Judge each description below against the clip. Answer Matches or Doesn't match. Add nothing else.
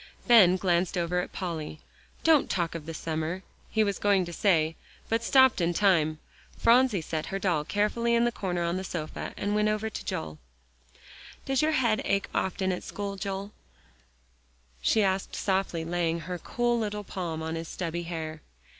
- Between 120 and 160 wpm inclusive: Doesn't match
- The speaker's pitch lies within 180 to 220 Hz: Matches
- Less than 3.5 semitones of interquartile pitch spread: Doesn't match